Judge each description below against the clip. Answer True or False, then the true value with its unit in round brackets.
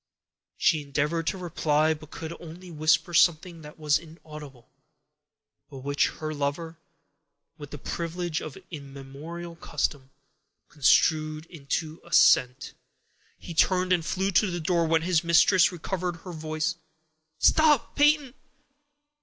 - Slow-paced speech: True (125 wpm)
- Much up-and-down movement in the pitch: False (2.6 semitones)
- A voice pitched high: False (160 Hz)